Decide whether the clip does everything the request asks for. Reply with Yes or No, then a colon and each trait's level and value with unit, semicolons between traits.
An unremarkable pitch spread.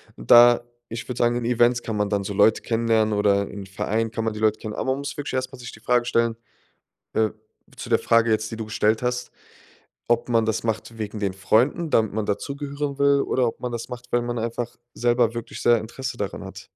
No: narrow, 2.1 semitones